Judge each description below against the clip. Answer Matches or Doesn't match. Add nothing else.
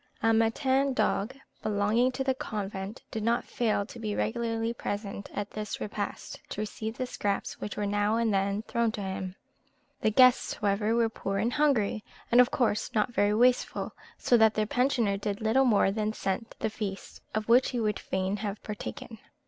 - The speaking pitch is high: Matches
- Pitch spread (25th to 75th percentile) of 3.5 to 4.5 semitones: Doesn't match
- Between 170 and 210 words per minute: Matches